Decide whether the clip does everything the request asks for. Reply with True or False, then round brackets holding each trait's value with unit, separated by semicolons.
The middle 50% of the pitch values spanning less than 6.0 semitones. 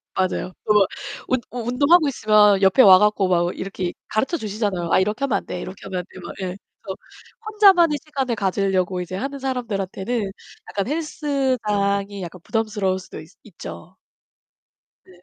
True (5.3 semitones)